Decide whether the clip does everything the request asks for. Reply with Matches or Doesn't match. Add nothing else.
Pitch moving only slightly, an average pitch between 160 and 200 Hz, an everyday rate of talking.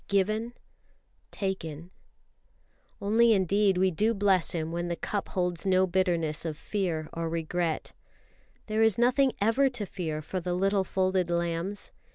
Doesn't match